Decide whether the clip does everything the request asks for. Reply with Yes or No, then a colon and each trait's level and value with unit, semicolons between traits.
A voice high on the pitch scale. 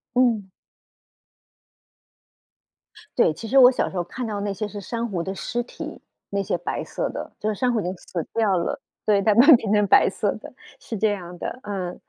Yes: high, 205 Hz